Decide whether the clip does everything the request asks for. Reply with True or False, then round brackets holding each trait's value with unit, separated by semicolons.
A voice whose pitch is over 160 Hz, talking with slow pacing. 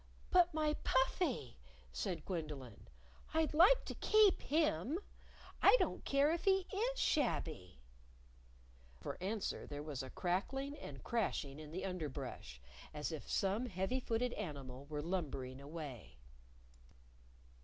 True (185 Hz; 125 wpm)